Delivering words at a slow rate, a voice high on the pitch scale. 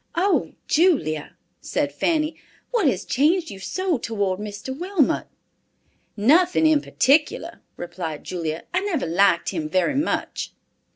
Yes: slow, 125 wpm; very high, 270 Hz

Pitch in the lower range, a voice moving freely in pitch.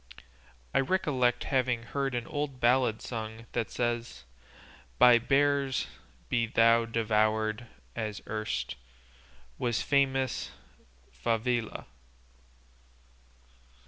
No: low, 120 Hz; narrow, 2.6 semitones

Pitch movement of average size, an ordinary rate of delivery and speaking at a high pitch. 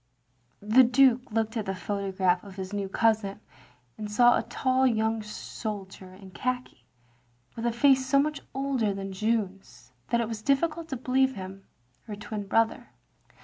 Yes: average, 4.4 semitones; average, 160 wpm; high, 220 Hz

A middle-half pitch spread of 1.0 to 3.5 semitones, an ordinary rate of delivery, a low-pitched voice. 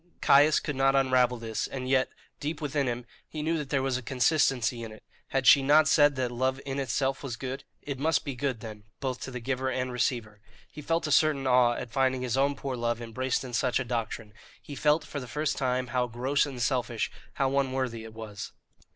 No: narrow, 2.4 semitones; fast, 220 wpm; low, 130 Hz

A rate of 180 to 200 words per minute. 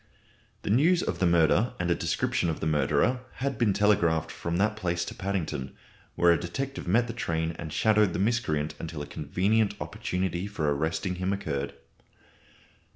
No: average, 170 wpm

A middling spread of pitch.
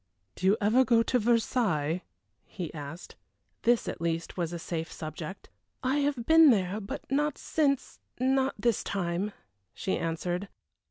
No: wide, 6.7 semitones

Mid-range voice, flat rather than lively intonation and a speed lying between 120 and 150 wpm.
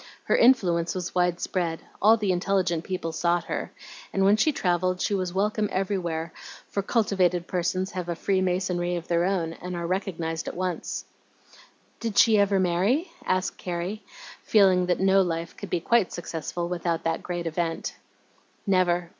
No: medium, 180 Hz; narrow, 2.1 semitones; average, 165 wpm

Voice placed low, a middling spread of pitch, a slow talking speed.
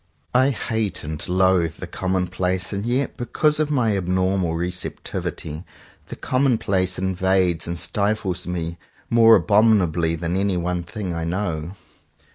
Yes: very low, 95 Hz; average, 3.5 semitones; slow, 130 wpm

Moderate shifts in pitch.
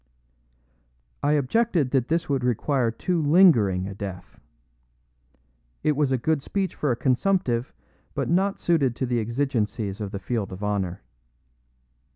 No: wide, 6.2 semitones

